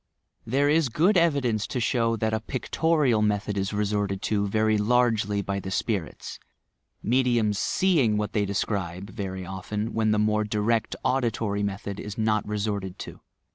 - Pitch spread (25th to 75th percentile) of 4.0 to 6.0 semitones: No, narrow, 2.6 semitones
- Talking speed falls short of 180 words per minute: Yes, average, 155 wpm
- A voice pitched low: Yes, low, 105 Hz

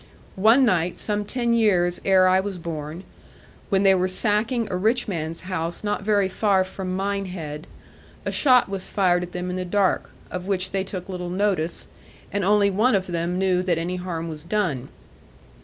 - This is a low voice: No, medium, 185 Hz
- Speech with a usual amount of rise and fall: No, narrow, 2.3 semitones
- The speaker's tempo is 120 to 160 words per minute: No, average, 185 wpm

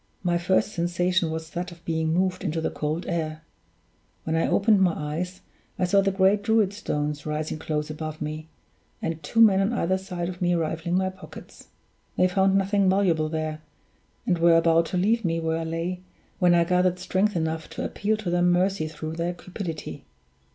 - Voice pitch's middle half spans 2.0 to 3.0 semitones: Yes, average, 2.7 semitones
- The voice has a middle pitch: Yes, medium, 175 Hz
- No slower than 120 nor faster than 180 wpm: No, average, 190 wpm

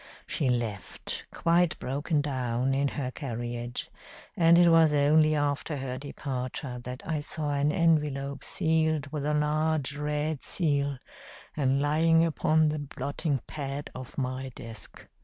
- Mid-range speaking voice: Yes, medium, 145 Hz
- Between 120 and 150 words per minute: Yes, average, 140 wpm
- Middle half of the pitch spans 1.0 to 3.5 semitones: Yes, average, 2.8 semitones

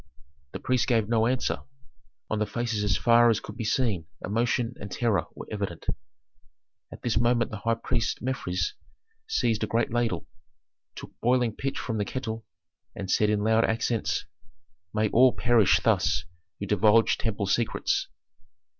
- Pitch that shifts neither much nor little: No, narrow, 2.3 semitones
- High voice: No, low, 115 Hz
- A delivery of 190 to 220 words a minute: No, average, 155 wpm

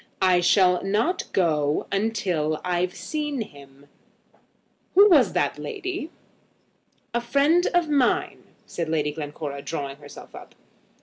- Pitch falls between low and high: Yes, medium, 180 Hz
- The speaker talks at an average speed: No, slow, 120 wpm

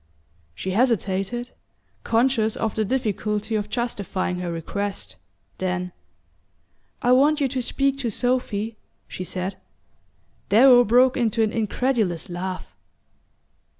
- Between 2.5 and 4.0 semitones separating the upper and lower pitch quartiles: No, average, 4.4 semitones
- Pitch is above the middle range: Yes, high, 220 Hz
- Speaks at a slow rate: Yes, slow, 115 wpm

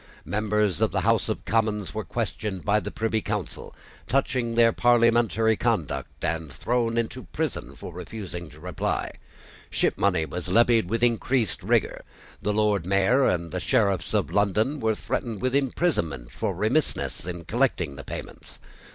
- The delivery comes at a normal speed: Yes, average, 150 wpm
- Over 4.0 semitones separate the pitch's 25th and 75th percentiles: Yes, average, 4.4 semitones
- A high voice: No, low, 105 Hz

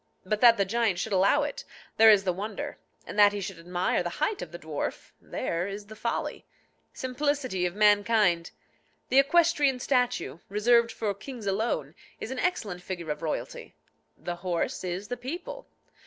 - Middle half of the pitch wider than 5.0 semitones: Yes, wide, 5.5 semitones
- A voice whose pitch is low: No, high, 210 Hz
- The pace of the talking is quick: No, average, 170 wpm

